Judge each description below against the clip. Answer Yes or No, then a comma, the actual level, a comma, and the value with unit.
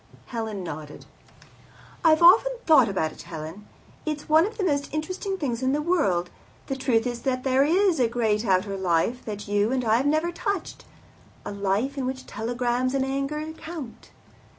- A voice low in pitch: No, very high, 255 Hz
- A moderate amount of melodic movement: No, wide, 6.6 semitones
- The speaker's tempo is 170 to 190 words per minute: Yes, average, 175 wpm